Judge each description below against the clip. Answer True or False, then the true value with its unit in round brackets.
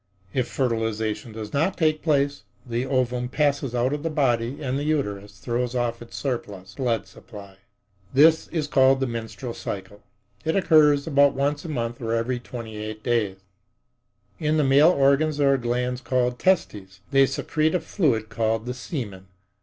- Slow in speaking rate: False (165 wpm)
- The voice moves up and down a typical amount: True (3.9 semitones)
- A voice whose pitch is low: True (125 Hz)